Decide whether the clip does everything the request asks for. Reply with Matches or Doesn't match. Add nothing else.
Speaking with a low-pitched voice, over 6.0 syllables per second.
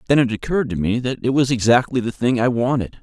Matches